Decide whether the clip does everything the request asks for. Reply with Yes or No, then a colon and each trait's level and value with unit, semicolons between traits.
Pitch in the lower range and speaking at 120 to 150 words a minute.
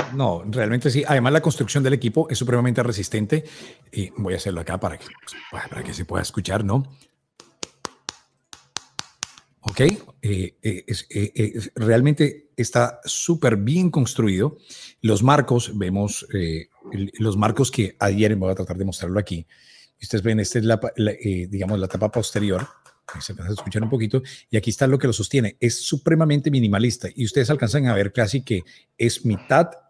No: low, 115 Hz; average, 170 wpm